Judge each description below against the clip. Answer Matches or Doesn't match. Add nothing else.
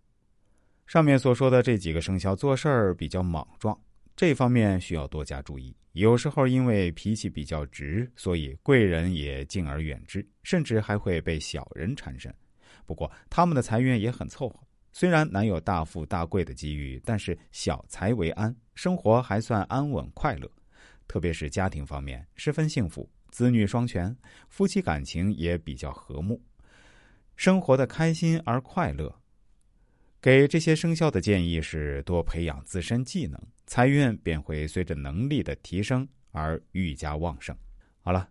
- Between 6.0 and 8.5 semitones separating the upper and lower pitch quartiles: Matches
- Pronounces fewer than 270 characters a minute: Matches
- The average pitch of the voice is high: Doesn't match